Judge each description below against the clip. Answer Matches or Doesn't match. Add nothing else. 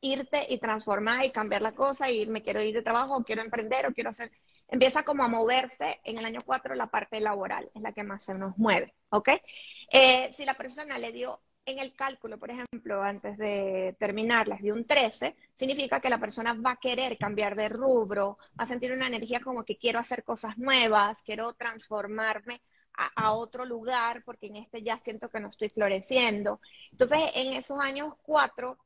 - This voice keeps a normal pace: Doesn't match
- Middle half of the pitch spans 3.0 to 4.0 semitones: Matches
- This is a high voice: Matches